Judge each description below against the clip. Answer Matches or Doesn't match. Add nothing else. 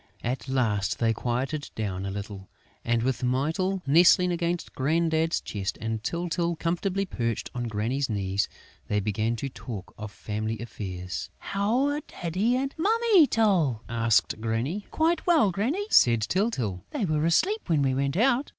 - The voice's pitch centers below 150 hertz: Matches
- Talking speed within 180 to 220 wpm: Doesn't match